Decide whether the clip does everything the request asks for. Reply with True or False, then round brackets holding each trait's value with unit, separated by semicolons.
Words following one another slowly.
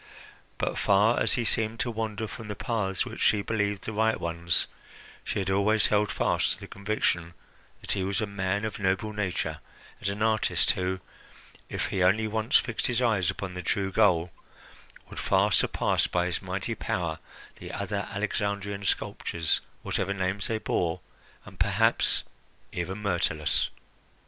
False (165 wpm)